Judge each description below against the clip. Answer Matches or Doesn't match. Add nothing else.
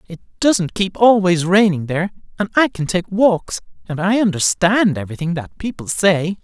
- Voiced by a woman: Doesn't match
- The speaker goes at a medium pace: Matches